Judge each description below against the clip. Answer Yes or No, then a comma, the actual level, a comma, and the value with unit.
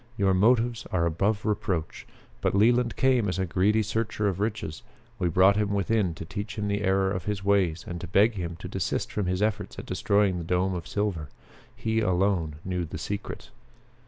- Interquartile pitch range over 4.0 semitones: No, average, 2.7 semitones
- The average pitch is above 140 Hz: No, low, 100 Hz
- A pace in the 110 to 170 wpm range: No, average, 195 wpm